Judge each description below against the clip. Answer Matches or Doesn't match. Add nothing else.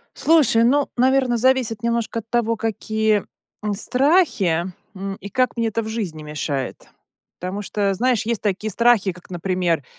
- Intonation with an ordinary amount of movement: Matches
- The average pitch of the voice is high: Matches